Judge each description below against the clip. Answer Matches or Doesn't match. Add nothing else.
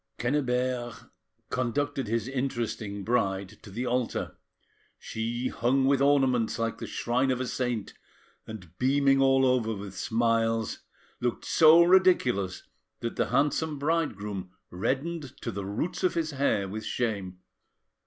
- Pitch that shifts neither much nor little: Matches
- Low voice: Matches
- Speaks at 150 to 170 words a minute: Doesn't match